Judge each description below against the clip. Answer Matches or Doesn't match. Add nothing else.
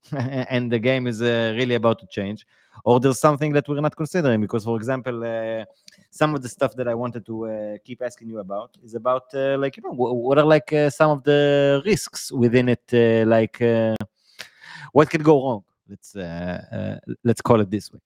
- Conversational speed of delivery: Doesn't match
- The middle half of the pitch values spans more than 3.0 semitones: Matches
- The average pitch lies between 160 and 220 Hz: Doesn't match